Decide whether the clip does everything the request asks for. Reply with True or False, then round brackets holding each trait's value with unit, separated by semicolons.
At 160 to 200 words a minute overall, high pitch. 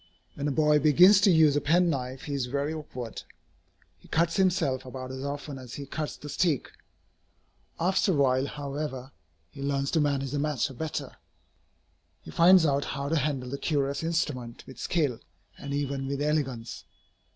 False (170 wpm; 140 Hz)